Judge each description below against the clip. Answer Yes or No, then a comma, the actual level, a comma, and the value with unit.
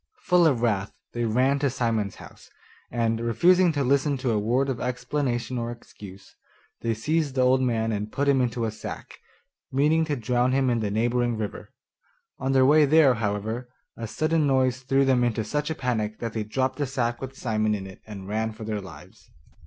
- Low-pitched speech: Yes, low, 125 Hz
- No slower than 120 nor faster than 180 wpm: No, average, 200 wpm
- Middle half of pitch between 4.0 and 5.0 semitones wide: No, average, 3.5 semitones